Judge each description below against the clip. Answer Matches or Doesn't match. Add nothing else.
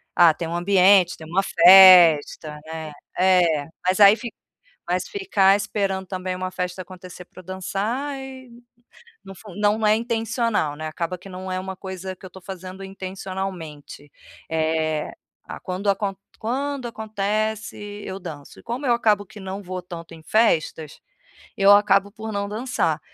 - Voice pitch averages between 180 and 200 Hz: Matches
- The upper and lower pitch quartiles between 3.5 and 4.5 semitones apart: Doesn't match